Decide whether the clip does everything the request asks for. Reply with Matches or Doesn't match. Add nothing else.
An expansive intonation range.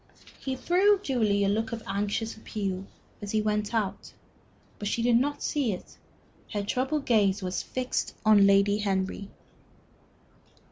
Doesn't match